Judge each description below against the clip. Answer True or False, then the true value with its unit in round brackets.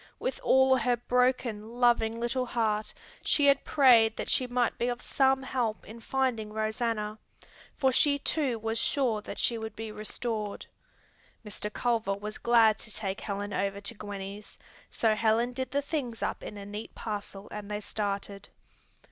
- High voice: True (225 Hz)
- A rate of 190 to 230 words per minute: False (165 wpm)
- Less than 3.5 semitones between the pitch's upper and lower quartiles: True (2.9 semitones)